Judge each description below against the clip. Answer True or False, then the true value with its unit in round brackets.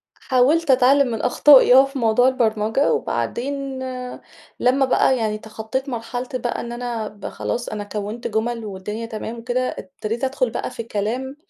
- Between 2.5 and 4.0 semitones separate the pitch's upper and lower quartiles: True (3.1 semitones)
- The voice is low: False (240 Hz)